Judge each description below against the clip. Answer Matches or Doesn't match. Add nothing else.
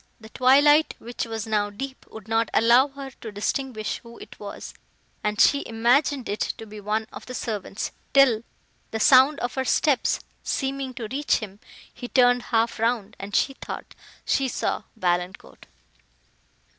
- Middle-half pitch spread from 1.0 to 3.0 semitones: Doesn't match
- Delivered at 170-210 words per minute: Doesn't match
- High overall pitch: Matches